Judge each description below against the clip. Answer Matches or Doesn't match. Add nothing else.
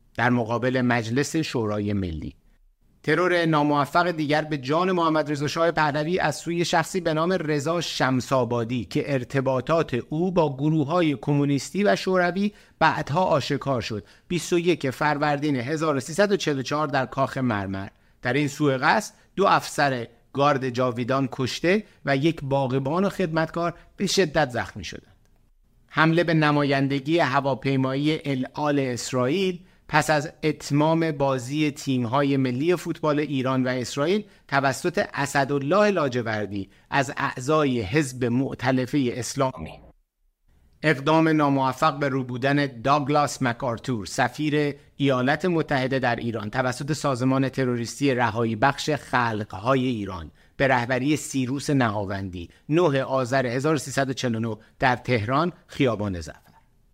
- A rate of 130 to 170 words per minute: Doesn't match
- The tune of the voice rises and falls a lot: Doesn't match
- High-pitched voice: Doesn't match